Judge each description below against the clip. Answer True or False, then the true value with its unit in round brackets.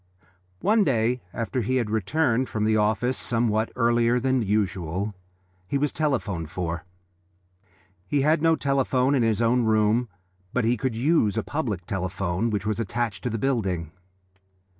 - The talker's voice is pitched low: True (115 Hz)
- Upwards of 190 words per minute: False (155 wpm)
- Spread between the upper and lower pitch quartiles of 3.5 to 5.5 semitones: True (3.8 semitones)